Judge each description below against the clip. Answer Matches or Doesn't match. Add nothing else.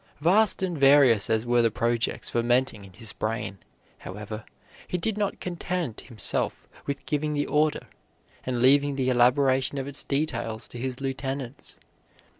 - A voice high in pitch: Doesn't match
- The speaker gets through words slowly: Doesn't match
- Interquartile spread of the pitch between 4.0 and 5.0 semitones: Doesn't match